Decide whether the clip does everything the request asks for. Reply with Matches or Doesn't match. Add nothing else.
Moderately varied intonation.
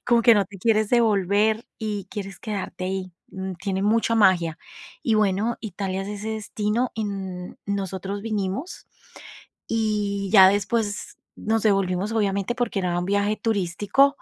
Doesn't match